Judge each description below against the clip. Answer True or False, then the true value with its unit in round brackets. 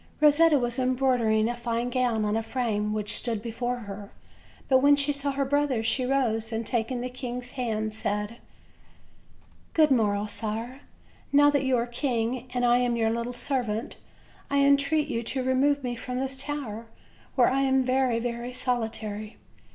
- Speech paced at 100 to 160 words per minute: False (170 wpm)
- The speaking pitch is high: True (245 Hz)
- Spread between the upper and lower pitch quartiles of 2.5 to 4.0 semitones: True (2.9 semitones)